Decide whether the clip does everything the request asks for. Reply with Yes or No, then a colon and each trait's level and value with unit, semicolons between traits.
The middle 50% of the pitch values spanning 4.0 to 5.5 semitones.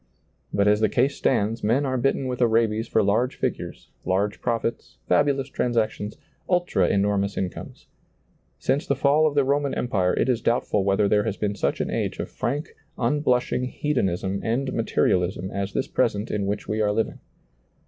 Yes: average, 4.4 semitones